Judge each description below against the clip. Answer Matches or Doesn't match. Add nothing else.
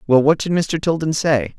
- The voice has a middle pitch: Matches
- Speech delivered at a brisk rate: Matches